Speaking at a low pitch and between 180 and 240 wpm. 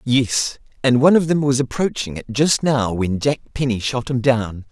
Yes: low, 125 Hz; fast, 205 wpm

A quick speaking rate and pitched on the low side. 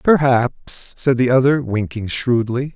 No: slow, 130 wpm; low, 125 Hz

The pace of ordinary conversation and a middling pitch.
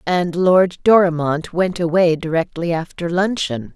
No: slow, 130 wpm; medium, 175 Hz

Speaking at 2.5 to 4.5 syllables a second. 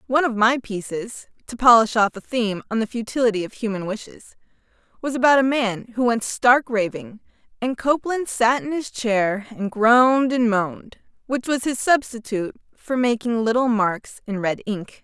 Yes: 3.9 syllables/s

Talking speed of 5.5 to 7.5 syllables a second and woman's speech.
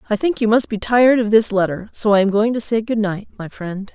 Yes: 5.8 syllables/s; female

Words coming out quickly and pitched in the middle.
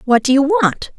No: fast, 245 wpm; very high, 270 Hz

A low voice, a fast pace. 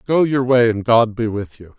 Yes: low, 120 Hz; fast, 270 wpm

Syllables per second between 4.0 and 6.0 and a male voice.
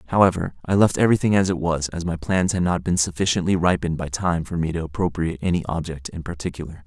No: 6.6 syllables/s; male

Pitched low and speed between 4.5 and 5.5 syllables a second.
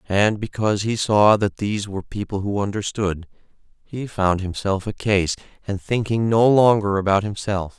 Yes: low, 105 Hz; 4.9 syllables/s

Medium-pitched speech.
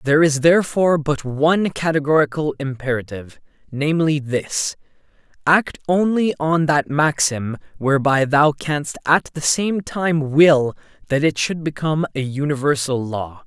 Yes: medium, 150 Hz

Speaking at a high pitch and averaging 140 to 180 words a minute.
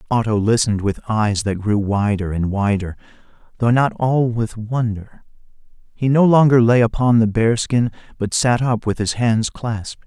No: low, 115 Hz; average, 175 wpm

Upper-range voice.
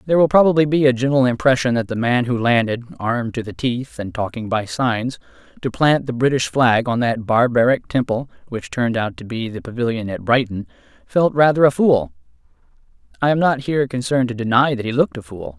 No: low, 125 Hz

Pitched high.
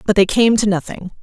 Yes: high, 205 Hz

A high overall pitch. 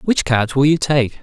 No: medium, 140 Hz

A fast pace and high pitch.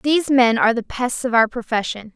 Yes: fast, 225 wpm; high, 240 Hz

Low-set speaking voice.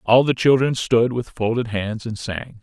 Yes: low, 115 Hz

